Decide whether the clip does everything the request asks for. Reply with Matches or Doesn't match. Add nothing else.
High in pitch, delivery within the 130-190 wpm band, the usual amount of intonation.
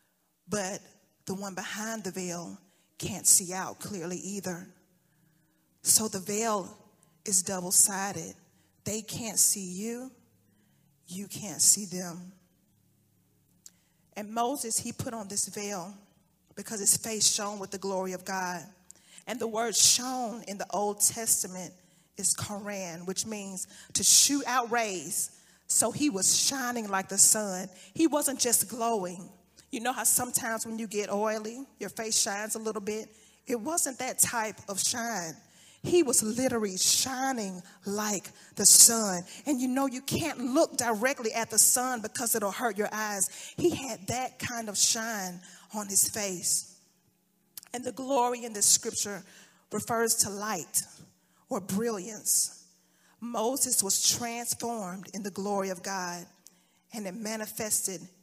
Matches